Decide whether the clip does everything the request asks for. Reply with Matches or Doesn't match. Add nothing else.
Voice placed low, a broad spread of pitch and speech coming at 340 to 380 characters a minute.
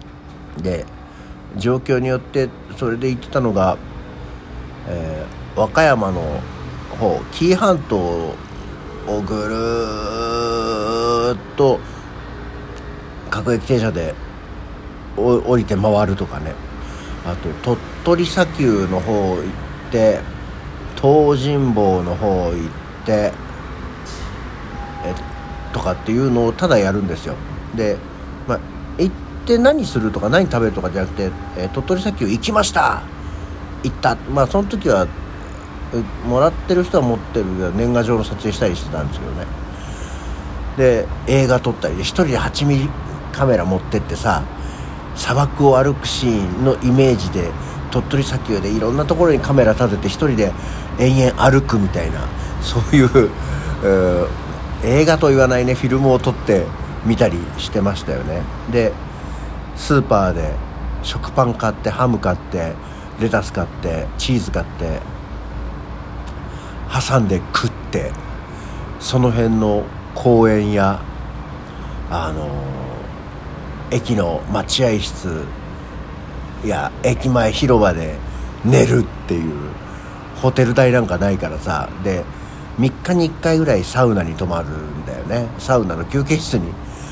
Doesn't match